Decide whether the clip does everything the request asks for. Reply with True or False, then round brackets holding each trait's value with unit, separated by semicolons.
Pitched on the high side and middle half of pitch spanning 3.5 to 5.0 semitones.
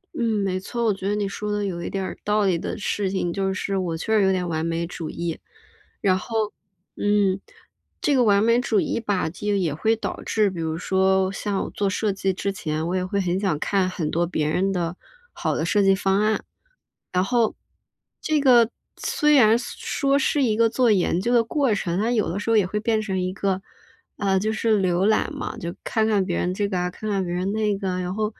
False (195 Hz; 2.9 semitones)